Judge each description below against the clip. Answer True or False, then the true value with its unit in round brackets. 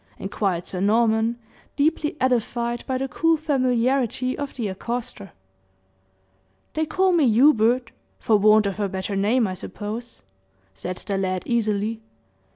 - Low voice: False (230 Hz)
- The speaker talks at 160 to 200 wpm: False (135 wpm)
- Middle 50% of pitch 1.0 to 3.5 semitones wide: False (4.0 semitones)